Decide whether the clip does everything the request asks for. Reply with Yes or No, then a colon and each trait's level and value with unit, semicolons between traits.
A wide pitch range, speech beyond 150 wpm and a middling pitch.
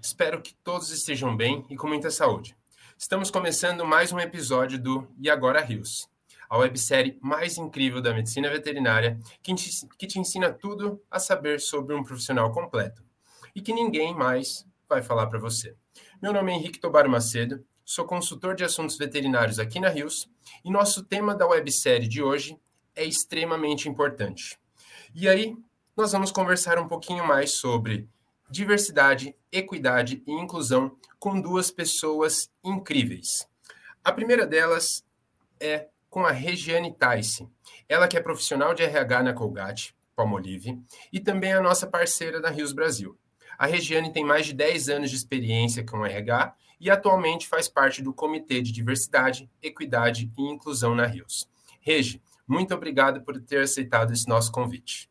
Yes: wide, 6.0 semitones; average, 160 wpm; medium, 145 Hz